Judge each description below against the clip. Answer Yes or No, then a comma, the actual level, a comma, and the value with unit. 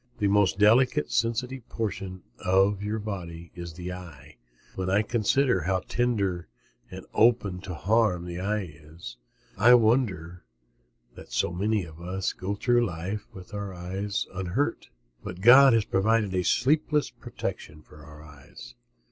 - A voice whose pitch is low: Yes, very low, 95 Hz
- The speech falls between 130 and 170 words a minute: Yes, average, 145 wpm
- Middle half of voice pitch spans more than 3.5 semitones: Yes, average, 4.0 semitones